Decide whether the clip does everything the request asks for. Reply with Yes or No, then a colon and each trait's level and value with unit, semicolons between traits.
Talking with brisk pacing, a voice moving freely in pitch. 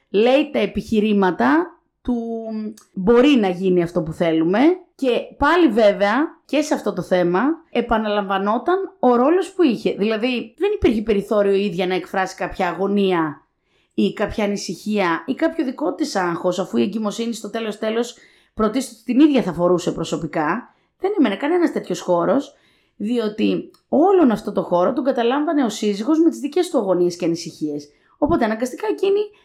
No: average, 155 wpm; wide, 7.3 semitones